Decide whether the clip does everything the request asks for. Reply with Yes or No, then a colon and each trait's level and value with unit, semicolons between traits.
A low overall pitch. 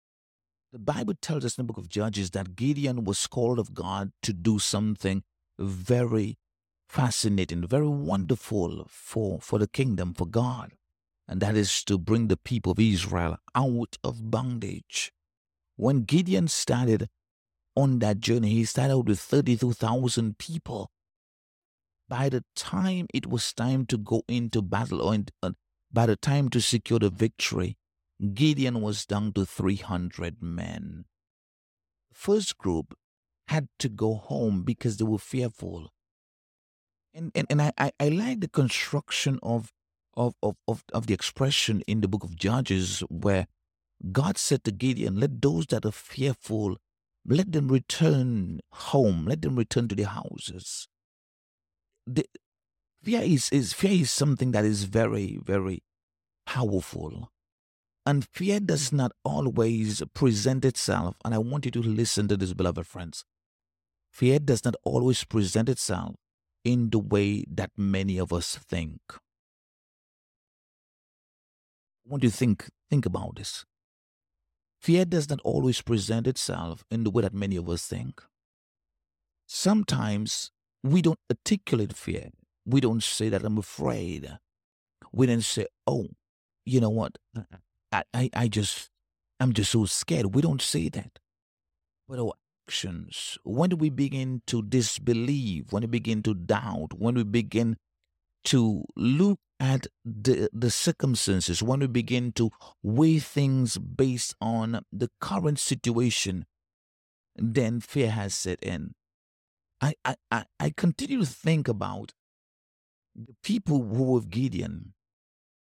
Yes: low, 110 Hz